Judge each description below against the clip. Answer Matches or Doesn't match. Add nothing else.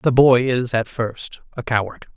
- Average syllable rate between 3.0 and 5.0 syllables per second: Matches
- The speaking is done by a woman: Doesn't match